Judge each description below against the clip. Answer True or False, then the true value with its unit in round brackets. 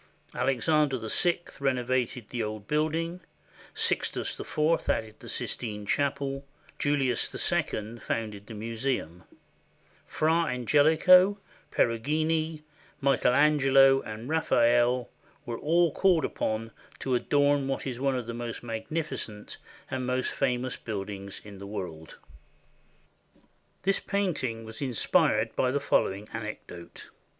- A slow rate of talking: True (115 wpm)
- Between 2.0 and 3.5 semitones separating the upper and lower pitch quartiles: False (5.1 semitones)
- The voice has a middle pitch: False (130 Hz)